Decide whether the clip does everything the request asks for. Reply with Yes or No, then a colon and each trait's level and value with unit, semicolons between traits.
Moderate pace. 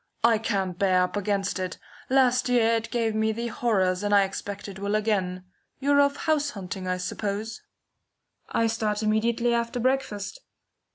Yes: average, 165 wpm